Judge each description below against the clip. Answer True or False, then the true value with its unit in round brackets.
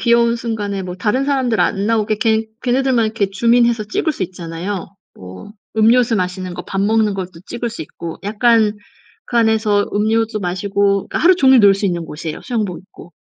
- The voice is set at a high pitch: True (215 Hz)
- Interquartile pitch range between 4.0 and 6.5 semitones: False (3.5 semitones)